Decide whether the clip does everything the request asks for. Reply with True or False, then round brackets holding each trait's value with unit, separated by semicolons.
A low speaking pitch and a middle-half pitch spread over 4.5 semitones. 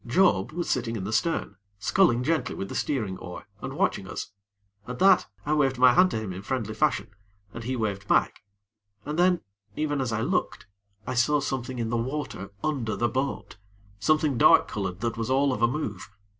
True (125 Hz; 5.1 semitones)